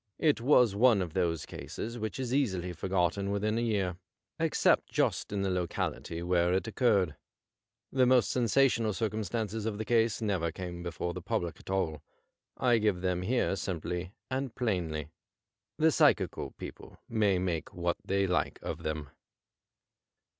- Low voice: Yes, low, 100 Hz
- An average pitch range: Yes, average, 4.5 semitones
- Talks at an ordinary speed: Yes, average, 155 wpm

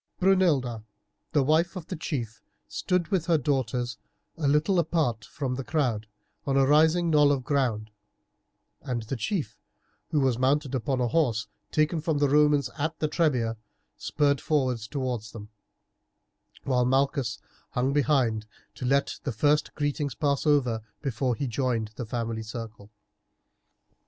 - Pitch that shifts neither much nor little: Yes, average, 4.0 semitones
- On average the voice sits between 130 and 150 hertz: Yes, low, 135 Hz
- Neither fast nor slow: Yes, average, 145 wpm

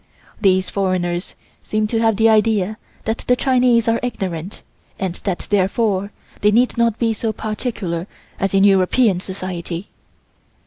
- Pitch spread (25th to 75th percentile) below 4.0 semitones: Yes, average, 3.4 semitones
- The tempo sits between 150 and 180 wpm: No, average, 140 wpm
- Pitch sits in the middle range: No, high, 205 Hz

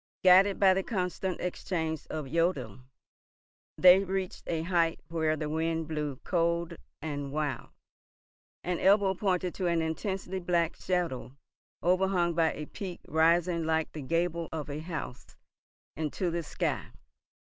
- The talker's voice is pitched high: No, medium, 170 Hz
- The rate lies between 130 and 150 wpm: Yes, slow, 135 wpm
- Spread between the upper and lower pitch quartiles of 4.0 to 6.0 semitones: No, narrow, 2.4 semitones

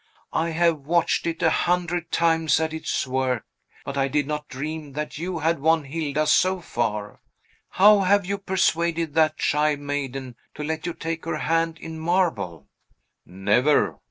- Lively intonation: No, average, 3.0 semitones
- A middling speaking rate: Yes, average, 160 wpm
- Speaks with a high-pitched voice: No, medium, 160 Hz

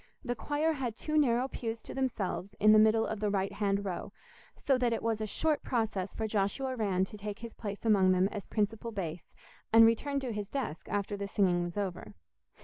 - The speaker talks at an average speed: No, fast, 215 wpm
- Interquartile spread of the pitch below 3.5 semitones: Yes, average, 3.0 semitones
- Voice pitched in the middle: No, high, 215 Hz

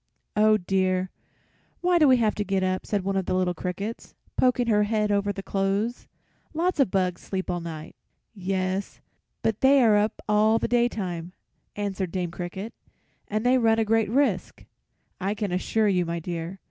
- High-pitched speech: Yes, high, 200 Hz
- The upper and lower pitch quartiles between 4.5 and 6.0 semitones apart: No, average, 3.2 semitones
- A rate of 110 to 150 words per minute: No, average, 170 wpm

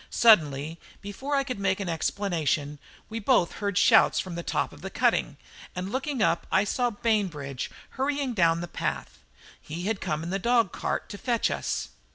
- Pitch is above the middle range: Yes, high, 195 Hz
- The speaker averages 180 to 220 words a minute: Yes, average, 185 wpm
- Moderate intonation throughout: No, wide, 5.8 semitones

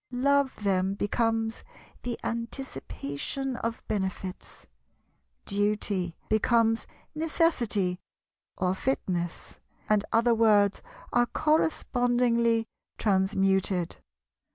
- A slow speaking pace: Yes, slow, 75 wpm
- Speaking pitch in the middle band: No, high, 220 Hz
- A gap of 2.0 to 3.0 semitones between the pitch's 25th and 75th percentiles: No, average, 4.0 semitones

